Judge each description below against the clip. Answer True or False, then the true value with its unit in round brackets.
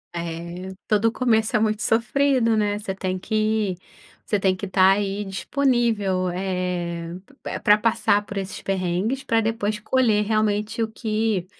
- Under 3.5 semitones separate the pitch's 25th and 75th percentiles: True (2.9 semitones)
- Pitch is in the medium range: False (210 Hz)